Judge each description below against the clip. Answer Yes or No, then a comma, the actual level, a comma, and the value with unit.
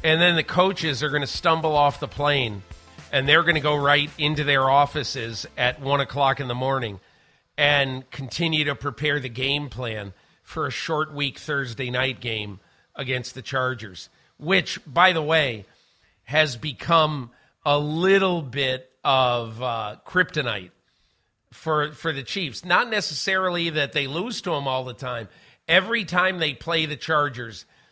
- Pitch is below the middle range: No, medium, 145 Hz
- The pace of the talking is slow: No, average, 160 wpm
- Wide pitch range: No, average, 3.8 semitones